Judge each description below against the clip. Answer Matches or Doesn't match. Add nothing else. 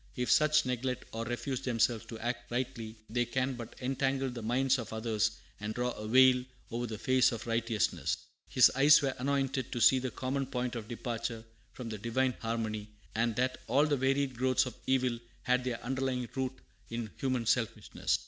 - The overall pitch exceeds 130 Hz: Doesn't match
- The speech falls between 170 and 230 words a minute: Matches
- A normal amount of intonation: Doesn't match